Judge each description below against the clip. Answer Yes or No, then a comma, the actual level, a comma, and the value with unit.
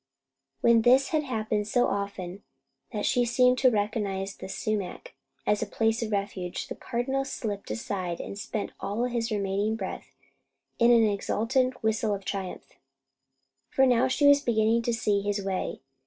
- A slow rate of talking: No, average, 160 wpm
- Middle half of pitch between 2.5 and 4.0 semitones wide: Yes, average, 3.3 semitones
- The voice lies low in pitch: No, high, 220 Hz